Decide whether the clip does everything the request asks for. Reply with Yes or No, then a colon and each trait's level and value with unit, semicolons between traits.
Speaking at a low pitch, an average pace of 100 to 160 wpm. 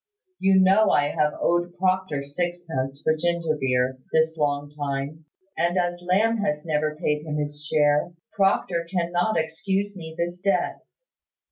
No: medium, 165 Hz; average, 145 wpm